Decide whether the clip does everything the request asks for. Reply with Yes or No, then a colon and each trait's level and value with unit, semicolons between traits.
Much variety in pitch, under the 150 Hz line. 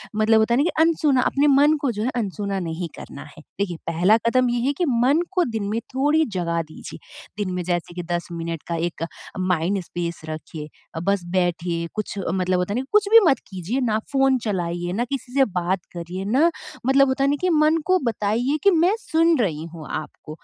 No: wide, 7.9 semitones; high, 205 Hz